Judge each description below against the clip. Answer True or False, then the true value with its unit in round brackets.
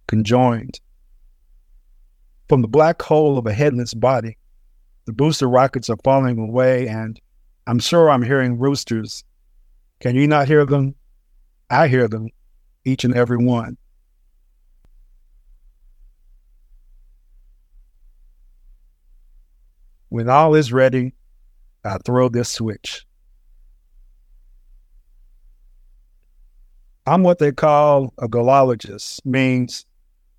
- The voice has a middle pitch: False (110 Hz)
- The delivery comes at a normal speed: False (95 wpm)